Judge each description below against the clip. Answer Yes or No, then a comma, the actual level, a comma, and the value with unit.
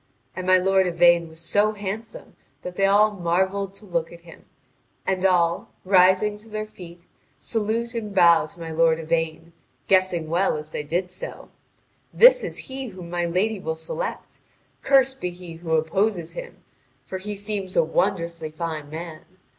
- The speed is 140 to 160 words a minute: No, average, 170 wpm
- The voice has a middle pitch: Yes, medium, 180 Hz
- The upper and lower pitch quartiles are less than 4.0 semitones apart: Yes, average, 3.5 semitones